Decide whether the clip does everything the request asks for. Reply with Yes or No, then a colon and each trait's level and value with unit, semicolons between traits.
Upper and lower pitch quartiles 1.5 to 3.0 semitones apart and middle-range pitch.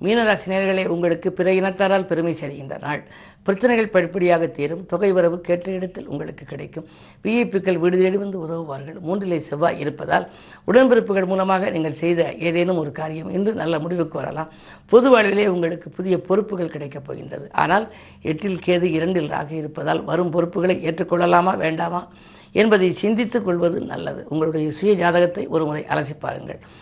Yes: average, 2.7 semitones; medium, 175 Hz